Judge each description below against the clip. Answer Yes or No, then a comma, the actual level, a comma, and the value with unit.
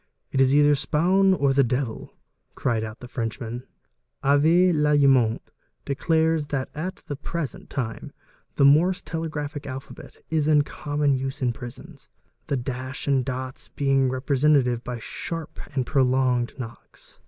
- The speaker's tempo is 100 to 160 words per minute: Yes, average, 140 wpm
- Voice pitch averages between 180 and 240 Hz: No, medium, 140 Hz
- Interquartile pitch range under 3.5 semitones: Yes, average, 2.9 semitones